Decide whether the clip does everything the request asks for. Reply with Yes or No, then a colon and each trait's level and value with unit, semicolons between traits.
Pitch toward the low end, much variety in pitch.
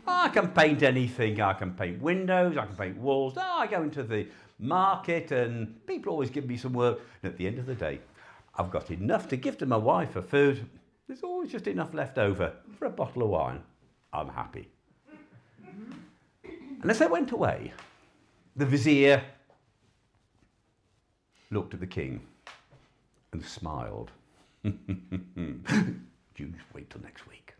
Yes: low, 130 Hz; wide, 8.5 semitones